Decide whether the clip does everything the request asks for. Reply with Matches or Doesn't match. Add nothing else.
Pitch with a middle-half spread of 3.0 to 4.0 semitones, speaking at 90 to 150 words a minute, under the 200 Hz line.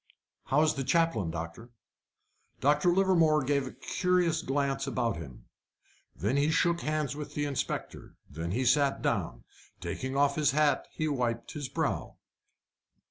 Matches